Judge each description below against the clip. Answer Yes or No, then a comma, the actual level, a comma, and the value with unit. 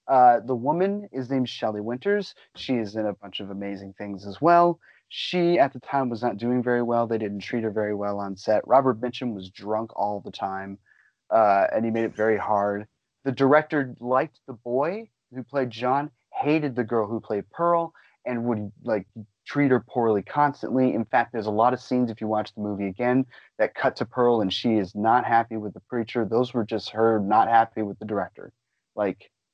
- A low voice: Yes, low, 120 Hz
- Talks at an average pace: No, fast, 210 wpm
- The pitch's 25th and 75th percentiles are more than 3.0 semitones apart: Yes, average, 3.5 semitones